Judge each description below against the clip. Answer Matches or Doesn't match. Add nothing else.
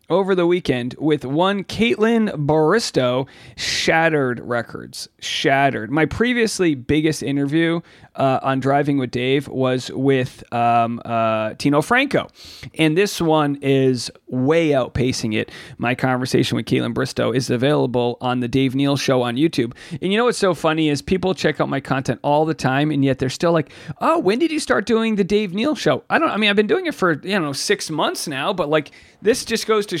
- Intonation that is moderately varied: Doesn't match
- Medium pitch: Matches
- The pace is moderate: Matches